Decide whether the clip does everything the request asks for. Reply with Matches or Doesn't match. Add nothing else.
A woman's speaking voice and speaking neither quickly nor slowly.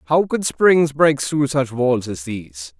Doesn't match